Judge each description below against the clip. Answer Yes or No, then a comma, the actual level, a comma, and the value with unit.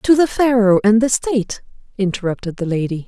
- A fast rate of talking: No, average, 175 wpm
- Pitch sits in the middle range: No, high, 220 Hz